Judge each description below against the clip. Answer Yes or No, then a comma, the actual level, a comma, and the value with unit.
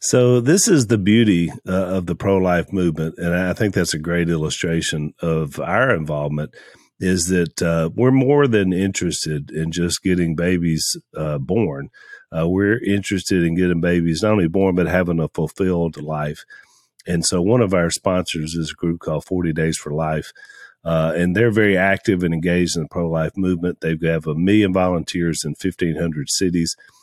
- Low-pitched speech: Yes, very low, 85 Hz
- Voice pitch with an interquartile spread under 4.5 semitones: Yes, average, 2.7 semitones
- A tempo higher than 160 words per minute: Yes, average, 180 wpm